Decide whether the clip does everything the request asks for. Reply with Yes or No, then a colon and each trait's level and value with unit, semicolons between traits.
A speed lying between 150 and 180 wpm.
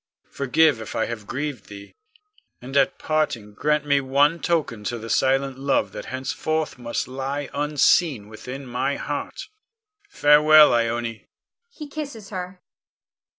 No: slow, 135 wpm